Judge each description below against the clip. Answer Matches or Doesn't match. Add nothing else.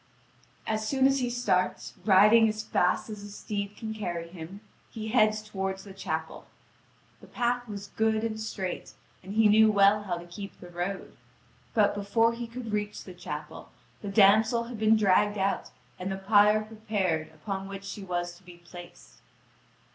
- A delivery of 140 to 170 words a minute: Doesn't match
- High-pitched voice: Matches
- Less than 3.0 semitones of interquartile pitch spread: Matches